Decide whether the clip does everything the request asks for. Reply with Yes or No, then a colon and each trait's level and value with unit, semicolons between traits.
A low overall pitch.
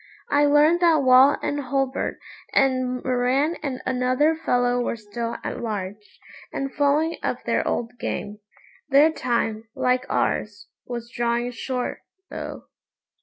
No: very high, 255 Hz